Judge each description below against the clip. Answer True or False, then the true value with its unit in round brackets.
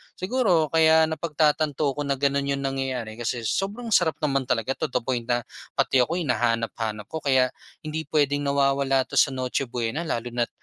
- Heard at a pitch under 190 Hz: True (140 Hz)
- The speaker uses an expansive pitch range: False (4.2 semitones)